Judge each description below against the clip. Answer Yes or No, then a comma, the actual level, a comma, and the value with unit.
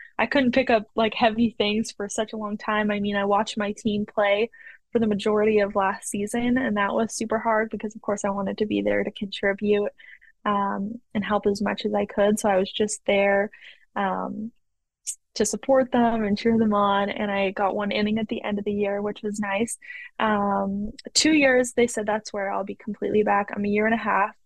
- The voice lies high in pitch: Yes, high, 210 Hz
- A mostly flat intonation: Yes, narrow, 1.7 semitones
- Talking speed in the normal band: No, fast, 225 wpm